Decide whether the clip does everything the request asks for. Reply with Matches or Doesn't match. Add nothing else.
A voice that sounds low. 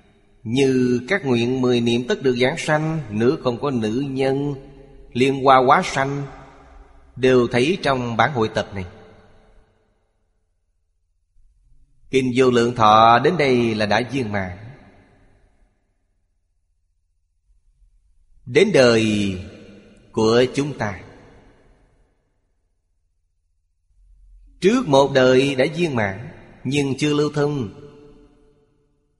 Matches